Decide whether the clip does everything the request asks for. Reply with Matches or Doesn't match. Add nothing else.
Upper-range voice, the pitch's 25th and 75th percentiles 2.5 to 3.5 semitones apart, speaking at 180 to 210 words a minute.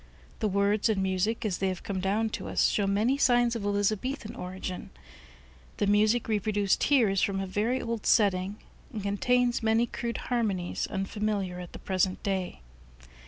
Doesn't match